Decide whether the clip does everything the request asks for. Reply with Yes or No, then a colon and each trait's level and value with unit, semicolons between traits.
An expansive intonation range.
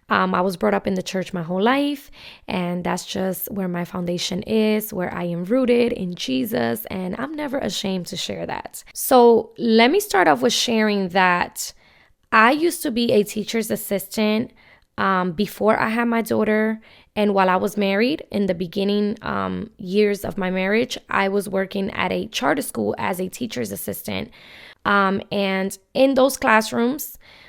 No: average, 3.7 semitones